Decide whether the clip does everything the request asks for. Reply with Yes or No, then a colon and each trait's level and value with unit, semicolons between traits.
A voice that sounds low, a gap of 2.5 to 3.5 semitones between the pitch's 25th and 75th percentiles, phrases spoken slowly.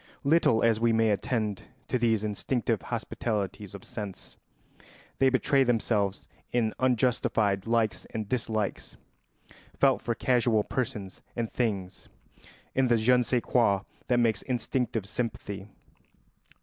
Yes: low, 115 Hz; average, 2.9 semitones; slow, 125 wpm